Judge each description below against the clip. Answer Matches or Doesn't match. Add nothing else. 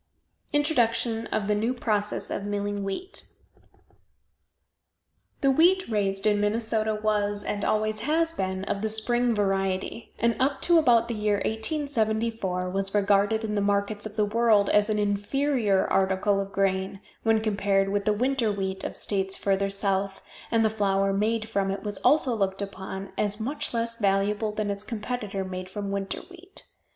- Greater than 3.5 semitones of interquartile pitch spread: Doesn't match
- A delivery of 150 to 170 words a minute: Matches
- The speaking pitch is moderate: Doesn't match